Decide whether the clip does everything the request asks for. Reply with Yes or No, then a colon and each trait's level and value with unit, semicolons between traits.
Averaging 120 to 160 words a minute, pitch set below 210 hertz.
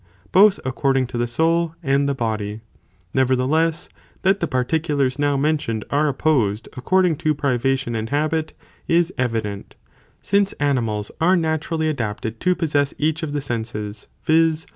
Yes: average, 140 wpm; medium, 140 Hz